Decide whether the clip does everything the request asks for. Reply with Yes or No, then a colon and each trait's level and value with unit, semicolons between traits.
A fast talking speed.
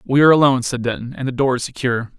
Yes: fast, 275 wpm